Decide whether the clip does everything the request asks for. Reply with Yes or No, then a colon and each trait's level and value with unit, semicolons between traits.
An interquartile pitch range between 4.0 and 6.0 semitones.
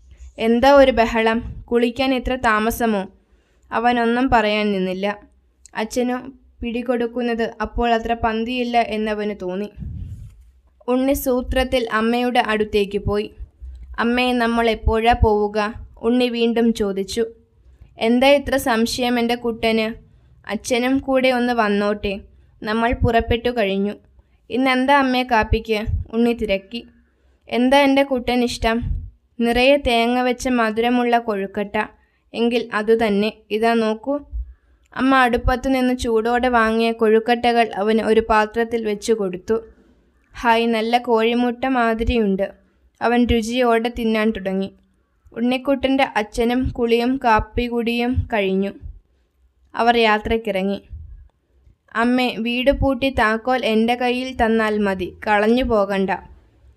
No: narrow, 2.6 semitones